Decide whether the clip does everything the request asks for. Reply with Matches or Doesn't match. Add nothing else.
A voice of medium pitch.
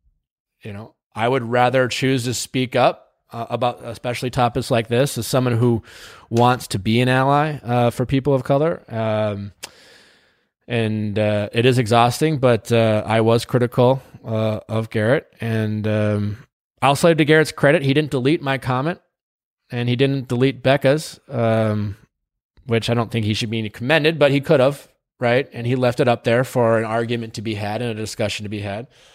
Doesn't match